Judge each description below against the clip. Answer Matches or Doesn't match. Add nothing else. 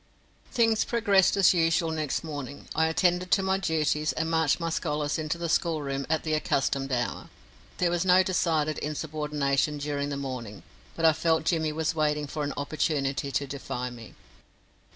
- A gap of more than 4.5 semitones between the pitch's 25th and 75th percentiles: Doesn't match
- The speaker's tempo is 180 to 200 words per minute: Doesn't match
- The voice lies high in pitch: Doesn't match